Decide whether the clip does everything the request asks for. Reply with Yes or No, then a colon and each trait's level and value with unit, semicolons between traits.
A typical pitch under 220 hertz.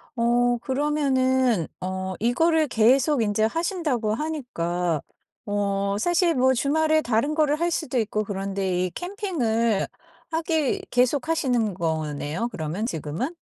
No: high, 240 Hz